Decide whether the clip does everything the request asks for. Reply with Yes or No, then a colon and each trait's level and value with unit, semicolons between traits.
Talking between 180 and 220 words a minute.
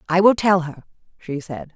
Yes: fast, 205 wpm